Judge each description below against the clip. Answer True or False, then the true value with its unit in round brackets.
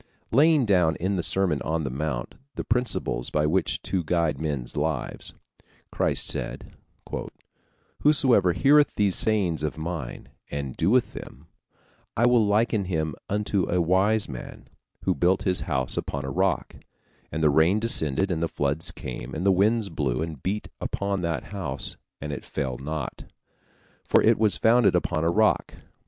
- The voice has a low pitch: True (90 Hz)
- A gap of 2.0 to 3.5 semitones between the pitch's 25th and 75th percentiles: False (5.1 semitones)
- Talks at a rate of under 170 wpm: True (160 wpm)